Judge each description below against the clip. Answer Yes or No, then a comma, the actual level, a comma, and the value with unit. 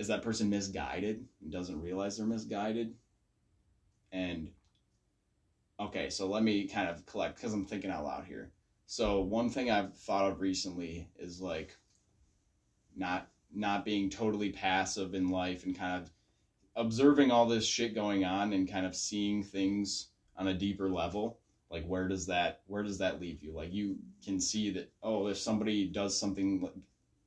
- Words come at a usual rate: Yes, average, 170 wpm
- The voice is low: Yes, low, 100 Hz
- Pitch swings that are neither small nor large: No, narrow, 2.0 semitones